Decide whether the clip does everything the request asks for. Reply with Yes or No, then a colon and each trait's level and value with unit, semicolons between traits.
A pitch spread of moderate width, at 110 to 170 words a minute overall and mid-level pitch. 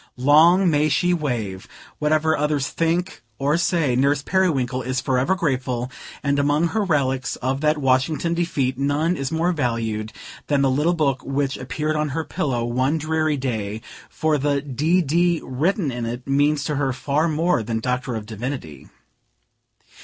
Yes: average, 3.6 semitones; average, 165 wpm; medium, 145 Hz